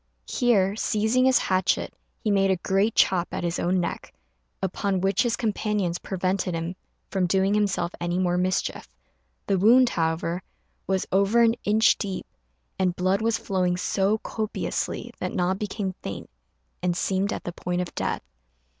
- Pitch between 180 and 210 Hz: Yes, high, 190 Hz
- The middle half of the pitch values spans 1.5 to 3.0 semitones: Yes, average, 2.7 semitones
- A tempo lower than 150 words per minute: No, average, 160 wpm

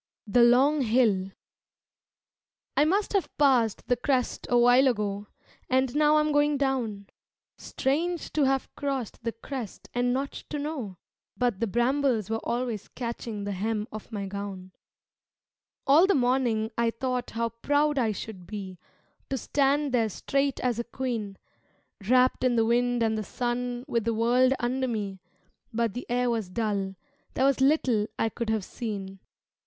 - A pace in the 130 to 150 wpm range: No, average, 160 wpm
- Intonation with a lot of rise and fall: No, average, 3.5 semitones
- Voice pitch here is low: No, high, 240 Hz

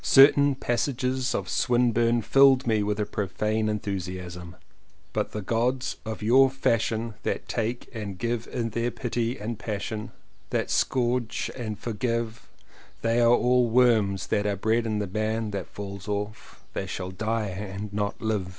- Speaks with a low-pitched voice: Yes, low, 110 Hz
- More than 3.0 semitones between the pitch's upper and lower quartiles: No, narrow, 2.6 semitones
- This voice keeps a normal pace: Yes, average, 160 wpm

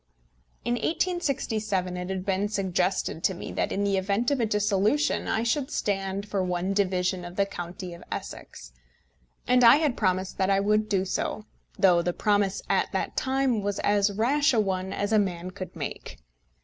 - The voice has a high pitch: Yes, high, 200 Hz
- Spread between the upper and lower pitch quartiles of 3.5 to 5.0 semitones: No, average, 3.0 semitones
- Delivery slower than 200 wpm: Yes, average, 185 wpm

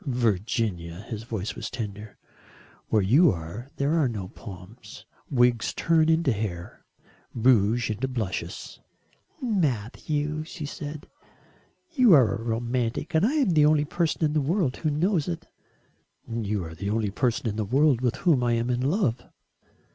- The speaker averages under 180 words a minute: Yes, average, 160 wpm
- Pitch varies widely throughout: Yes, wide, 5.9 semitones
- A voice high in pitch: No, low, 120 Hz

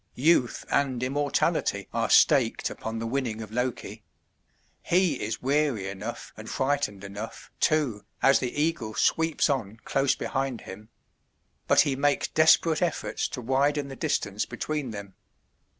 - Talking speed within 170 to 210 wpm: No, average, 140 wpm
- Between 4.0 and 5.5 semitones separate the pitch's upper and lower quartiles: Yes, average, 4.6 semitones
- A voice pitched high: No, low, 130 Hz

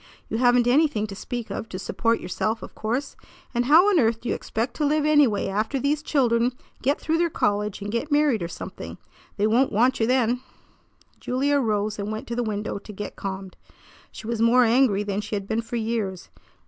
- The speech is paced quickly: Yes, fast, 210 wpm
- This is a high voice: Yes, high, 230 Hz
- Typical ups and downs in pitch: Yes, average, 3.8 semitones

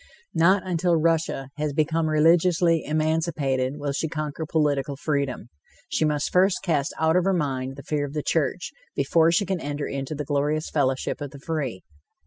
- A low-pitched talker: No, medium, 155 Hz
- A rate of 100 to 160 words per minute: No, average, 175 wpm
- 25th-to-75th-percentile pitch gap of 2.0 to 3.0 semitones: Yes, average, 2.7 semitones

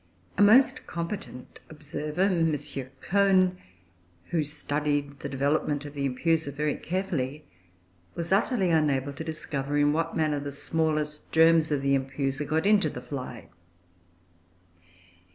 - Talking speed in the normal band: No, slow, 130 wpm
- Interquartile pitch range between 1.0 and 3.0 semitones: Yes, average, 2.7 semitones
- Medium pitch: Yes, medium, 150 Hz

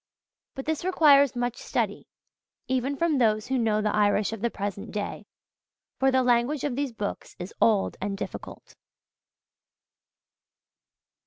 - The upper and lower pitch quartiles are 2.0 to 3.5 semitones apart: No, average, 4.2 semitones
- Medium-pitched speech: No, high, 240 Hz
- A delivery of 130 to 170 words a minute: Yes, average, 140 wpm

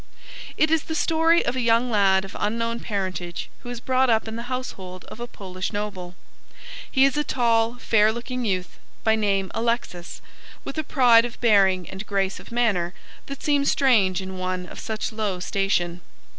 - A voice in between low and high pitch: No, high, 220 Hz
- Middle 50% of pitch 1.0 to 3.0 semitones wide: No, average, 4.3 semitones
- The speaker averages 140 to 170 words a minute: No, average, 185 wpm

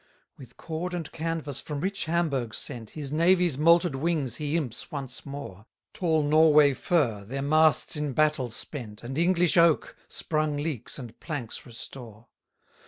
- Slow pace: No, average, 155 wpm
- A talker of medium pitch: Yes, medium, 150 Hz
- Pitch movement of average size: Yes, average, 4.0 semitones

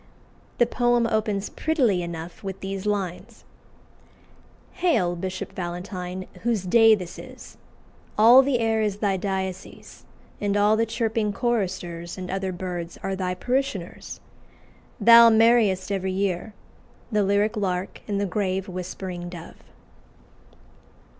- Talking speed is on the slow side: Yes, slow, 125 wpm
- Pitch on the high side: Yes, high, 195 Hz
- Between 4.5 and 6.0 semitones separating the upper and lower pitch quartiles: No, average, 3.4 semitones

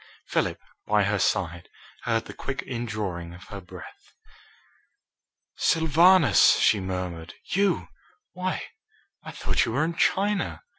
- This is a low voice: Yes, low, 110 Hz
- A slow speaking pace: Yes, slow, 120 wpm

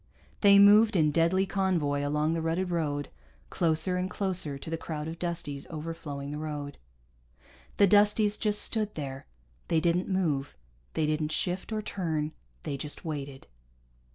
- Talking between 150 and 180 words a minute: Yes, average, 155 wpm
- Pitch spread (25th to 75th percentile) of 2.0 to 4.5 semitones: Yes, average, 4.0 semitones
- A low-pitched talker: No, medium, 165 Hz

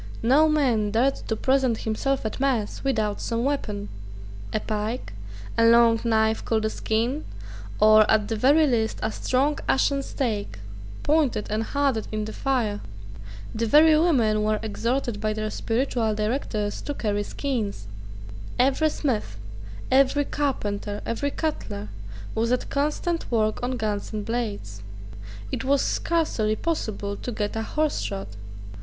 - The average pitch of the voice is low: No, high, 230 Hz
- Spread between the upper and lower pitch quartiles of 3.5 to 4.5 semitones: Yes, average, 4.2 semitones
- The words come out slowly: No, average, 145 wpm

